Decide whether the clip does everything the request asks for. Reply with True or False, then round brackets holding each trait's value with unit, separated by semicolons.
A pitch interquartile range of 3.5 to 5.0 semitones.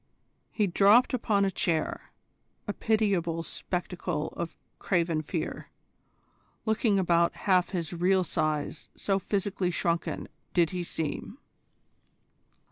False (3.0 semitones)